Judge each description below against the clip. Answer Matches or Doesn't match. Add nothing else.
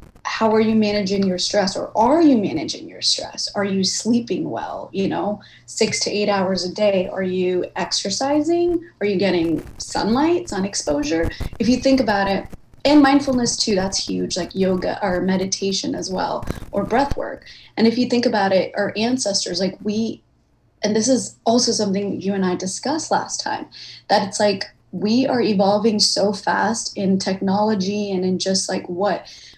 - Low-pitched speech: Doesn't match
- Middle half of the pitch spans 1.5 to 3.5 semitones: Matches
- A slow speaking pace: Doesn't match